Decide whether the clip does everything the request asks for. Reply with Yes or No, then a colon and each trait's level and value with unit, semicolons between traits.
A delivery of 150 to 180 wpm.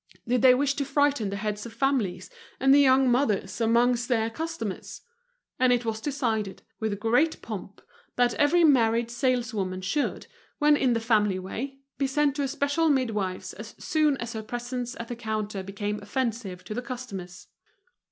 Yes: average, 170 wpm